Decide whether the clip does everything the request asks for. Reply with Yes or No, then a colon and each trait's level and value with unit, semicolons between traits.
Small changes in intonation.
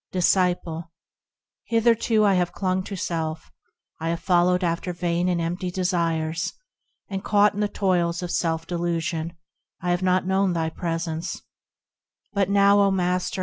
Yes: narrow, 2.2 semitones